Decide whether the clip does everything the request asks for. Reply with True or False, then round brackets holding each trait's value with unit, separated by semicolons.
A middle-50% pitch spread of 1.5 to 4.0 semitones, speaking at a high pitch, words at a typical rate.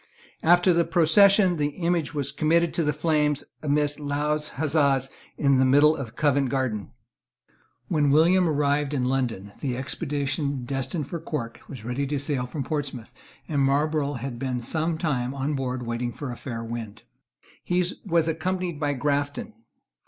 False (3.1 semitones; 145 Hz; 160 wpm)